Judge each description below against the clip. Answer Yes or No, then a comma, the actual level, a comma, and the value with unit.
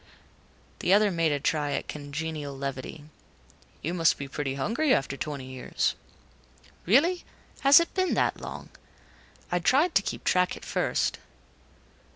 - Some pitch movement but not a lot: No, wide, 7.2 semitones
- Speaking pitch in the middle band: Yes, medium, 160 Hz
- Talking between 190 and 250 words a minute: No, average, 145 wpm